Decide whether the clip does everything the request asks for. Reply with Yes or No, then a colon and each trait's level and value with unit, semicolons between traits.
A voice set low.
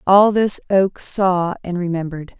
No: medium, 185 Hz